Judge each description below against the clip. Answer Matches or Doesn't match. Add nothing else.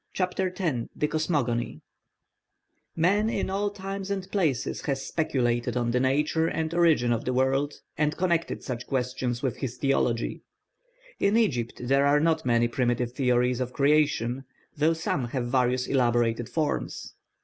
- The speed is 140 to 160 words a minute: Matches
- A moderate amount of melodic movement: Matches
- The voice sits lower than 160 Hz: Matches